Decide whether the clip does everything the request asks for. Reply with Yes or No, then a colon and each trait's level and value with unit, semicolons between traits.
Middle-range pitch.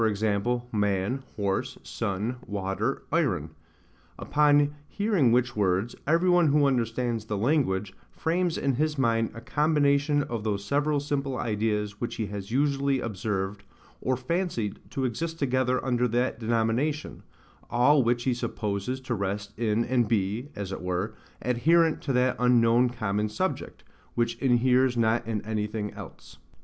No: low, 120 Hz